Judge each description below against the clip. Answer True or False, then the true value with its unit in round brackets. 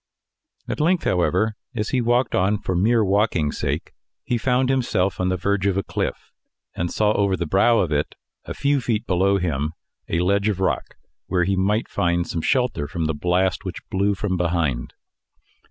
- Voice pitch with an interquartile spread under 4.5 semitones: True (3.7 semitones)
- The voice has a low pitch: True (95 Hz)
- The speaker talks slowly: False (185 wpm)